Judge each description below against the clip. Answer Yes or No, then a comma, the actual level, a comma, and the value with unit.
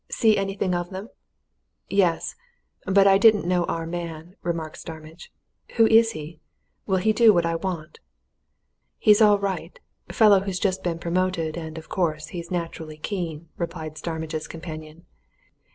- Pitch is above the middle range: No, medium, 175 Hz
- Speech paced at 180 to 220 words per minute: No, average, 150 wpm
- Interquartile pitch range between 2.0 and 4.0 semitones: Yes, average, 3.4 semitones